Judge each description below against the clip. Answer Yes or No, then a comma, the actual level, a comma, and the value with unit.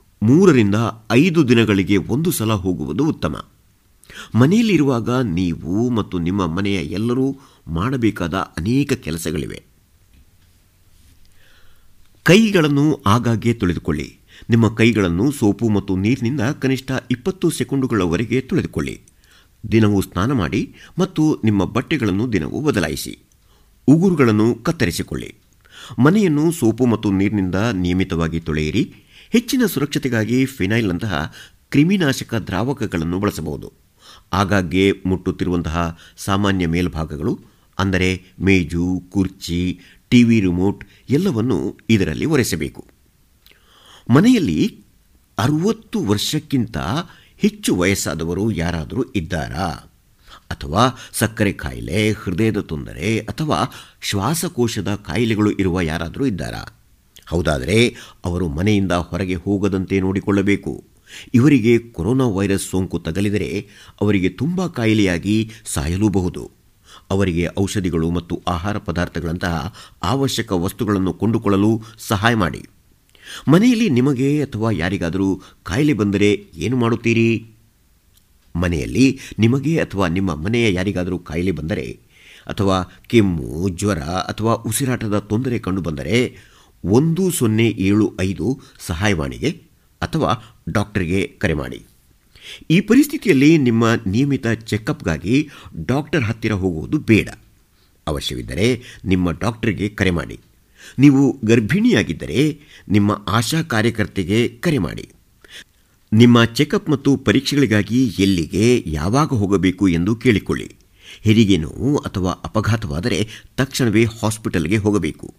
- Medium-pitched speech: No, low, 105 Hz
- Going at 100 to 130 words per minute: No, average, 90 wpm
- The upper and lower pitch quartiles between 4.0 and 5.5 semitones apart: Yes, average, 4.7 semitones